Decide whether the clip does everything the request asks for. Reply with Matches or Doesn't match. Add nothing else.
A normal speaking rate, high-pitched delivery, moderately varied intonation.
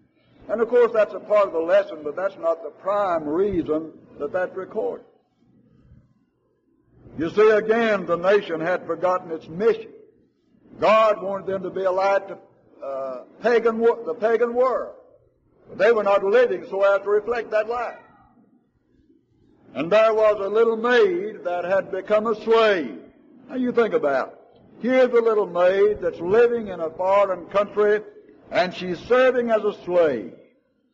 Matches